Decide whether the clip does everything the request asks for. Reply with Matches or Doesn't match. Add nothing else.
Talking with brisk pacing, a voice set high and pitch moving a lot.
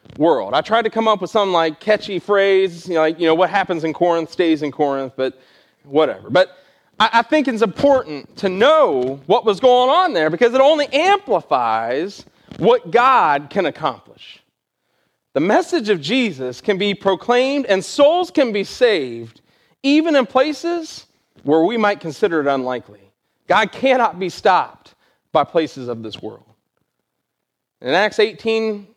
Doesn't match